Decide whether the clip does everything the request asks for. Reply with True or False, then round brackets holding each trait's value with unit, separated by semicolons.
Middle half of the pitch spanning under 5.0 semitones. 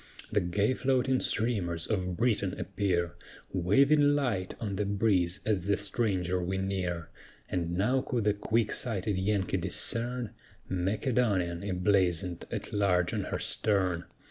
True (3.6 semitones)